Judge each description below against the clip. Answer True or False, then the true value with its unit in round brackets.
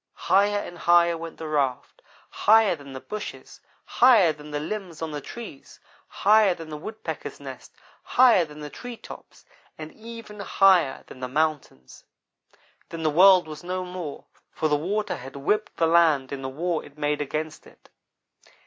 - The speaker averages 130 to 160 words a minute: False (170 wpm)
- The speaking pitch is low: False (165 Hz)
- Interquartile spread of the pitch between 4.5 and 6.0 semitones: True (4.9 semitones)